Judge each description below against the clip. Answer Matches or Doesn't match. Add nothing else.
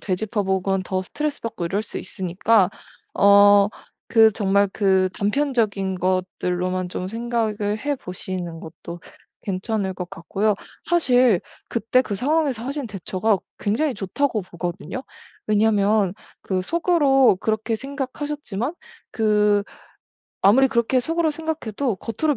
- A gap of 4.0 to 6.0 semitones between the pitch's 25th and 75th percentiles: Matches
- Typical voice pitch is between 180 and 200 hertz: Doesn't match